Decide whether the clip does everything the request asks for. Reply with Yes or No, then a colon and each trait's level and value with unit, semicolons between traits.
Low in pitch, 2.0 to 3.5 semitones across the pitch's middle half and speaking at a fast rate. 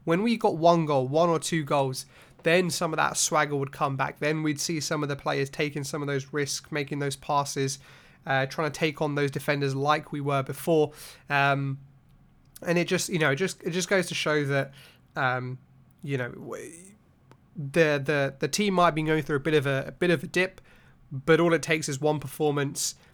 No: medium, 150 Hz; average, 2.8 semitones; fast, 220 wpm